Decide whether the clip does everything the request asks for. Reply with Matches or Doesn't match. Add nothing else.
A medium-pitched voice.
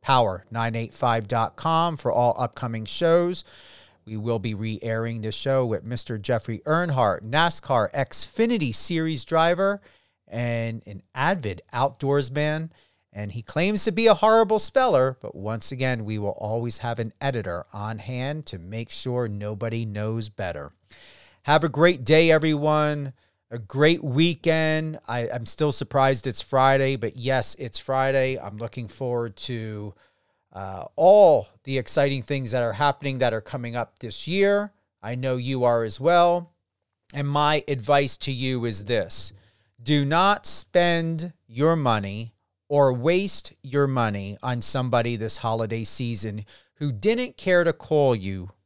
Doesn't match